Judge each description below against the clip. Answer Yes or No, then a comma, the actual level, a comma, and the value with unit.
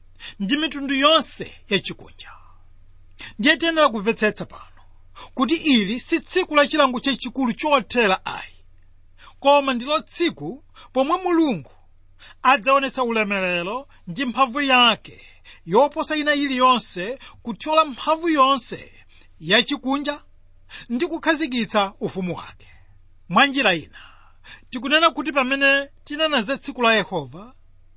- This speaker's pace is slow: Yes, slow, 100 wpm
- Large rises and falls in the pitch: Yes, wide, 8.7 semitones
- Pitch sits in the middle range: No, very high, 255 Hz